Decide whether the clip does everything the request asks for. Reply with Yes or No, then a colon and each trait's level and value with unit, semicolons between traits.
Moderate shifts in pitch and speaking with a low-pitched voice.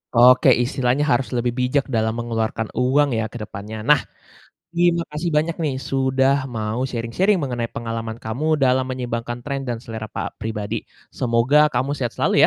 Yes: average, 3.3 semitones; low, 125 Hz